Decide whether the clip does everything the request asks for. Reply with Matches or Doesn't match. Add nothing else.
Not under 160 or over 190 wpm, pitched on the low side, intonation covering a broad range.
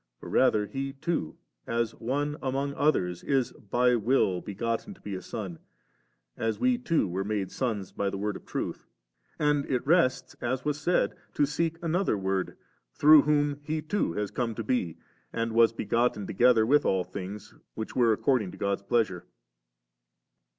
Matches